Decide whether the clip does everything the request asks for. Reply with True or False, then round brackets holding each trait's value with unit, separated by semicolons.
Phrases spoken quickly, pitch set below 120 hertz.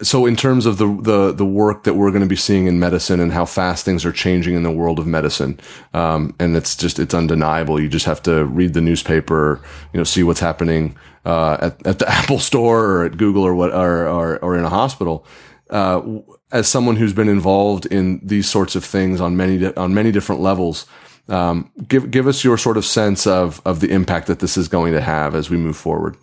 True (230 wpm; 90 Hz)